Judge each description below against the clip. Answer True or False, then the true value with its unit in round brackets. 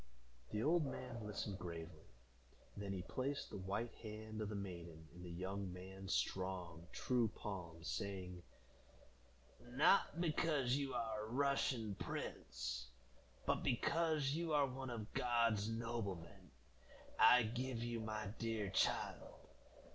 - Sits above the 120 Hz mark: False (110 Hz)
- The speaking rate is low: True (130 wpm)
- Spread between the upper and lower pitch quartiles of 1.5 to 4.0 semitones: False (4.9 semitones)